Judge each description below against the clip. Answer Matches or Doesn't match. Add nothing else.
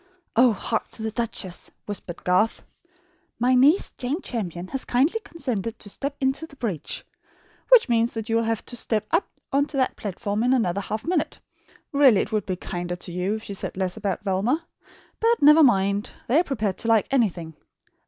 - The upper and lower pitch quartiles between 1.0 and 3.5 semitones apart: Doesn't match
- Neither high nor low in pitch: Doesn't match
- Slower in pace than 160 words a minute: Doesn't match